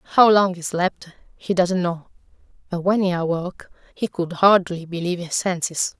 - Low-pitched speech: No, medium, 180 Hz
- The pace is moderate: Yes, average, 170 wpm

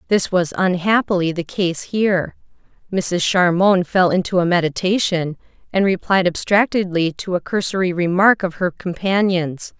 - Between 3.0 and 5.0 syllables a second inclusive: Yes, 4.6 syllables/s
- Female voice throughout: Yes, female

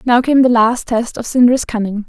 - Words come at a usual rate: No, fast, 230 wpm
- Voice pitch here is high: Yes, high, 240 Hz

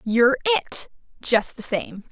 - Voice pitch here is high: Yes, very high, 250 Hz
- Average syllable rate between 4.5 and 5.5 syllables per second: Yes, 4.6 syllables/s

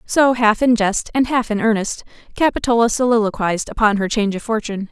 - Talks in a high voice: Yes, high, 225 Hz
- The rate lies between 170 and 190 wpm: Yes, average, 185 wpm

